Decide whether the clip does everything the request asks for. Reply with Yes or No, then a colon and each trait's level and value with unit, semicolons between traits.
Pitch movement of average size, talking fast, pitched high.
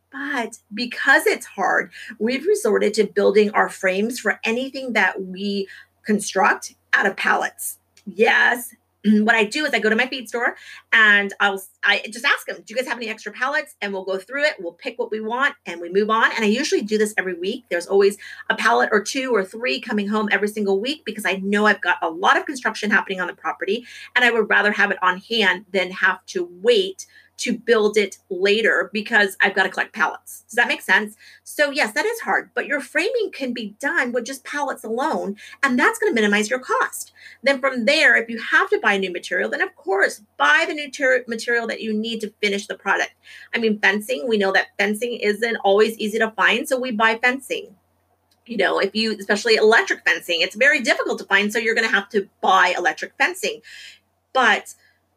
Yes: average, 4.7 semitones; fast, 220 wpm; high, 220 Hz